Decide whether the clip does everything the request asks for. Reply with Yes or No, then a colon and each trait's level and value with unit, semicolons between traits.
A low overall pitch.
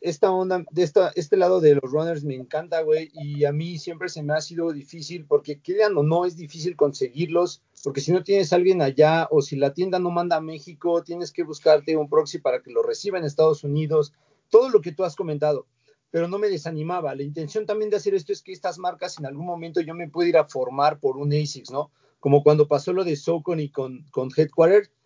No: medium, 165 Hz